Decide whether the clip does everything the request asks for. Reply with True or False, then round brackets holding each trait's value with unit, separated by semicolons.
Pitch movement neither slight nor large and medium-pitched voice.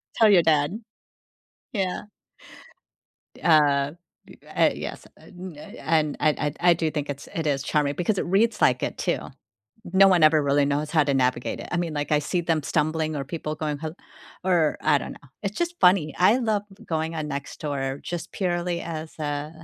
True (3.3 semitones; 155 Hz)